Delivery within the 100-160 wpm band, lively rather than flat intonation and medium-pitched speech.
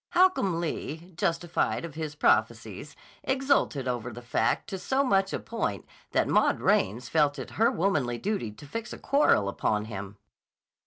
Yes: average, 155 wpm; wide, 8.6 semitones; medium, 160 Hz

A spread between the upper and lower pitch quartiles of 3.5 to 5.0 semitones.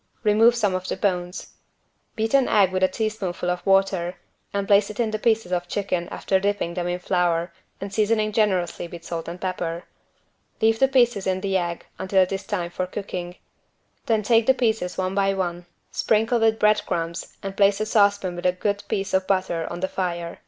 No: average, 3.0 semitones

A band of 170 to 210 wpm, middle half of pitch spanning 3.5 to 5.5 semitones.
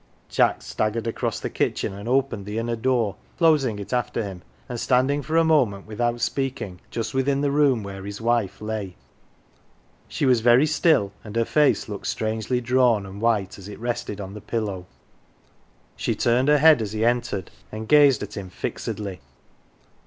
Yes: average, 175 wpm; average, 4.2 semitones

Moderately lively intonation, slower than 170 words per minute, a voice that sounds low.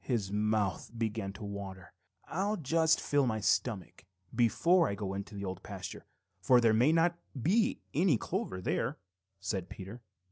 No: wide, 7.3 semitones; average, 155 wpm; low, 110 Hz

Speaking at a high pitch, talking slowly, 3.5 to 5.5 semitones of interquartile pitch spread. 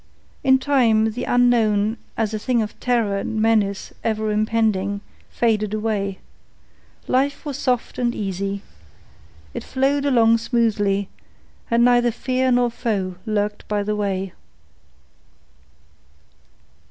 No: high, 220 Hz; slow, 115 wpm; average, 2.9 semitones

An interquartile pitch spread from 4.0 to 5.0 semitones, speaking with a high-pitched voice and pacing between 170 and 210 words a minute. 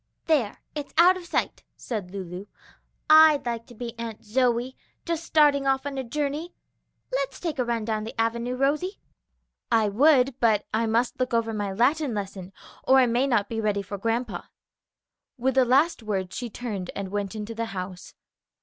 Yes: average, 4.5 semitones; high, 235 Hz; average, 180 wpm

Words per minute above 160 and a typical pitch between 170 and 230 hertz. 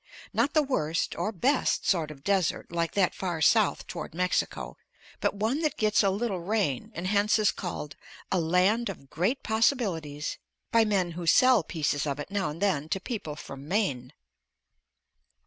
Yes: average, 170 wpm; medium, 185 Hz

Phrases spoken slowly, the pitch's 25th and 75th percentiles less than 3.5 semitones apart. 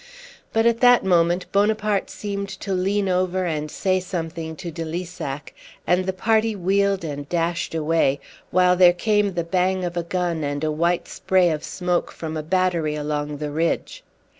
No: average, 175 wpm; average, 2.9 semitones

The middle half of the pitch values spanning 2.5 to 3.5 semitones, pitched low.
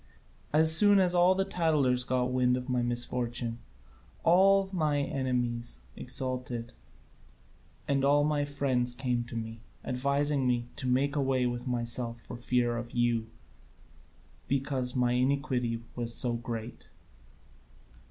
Yes: average, 2.8 semitones; low, 125 Hz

